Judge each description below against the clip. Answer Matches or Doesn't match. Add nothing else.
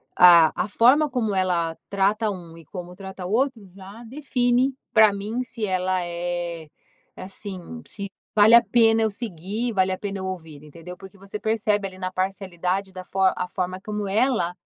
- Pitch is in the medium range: Doesn't match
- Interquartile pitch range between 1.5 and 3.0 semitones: Doesn't match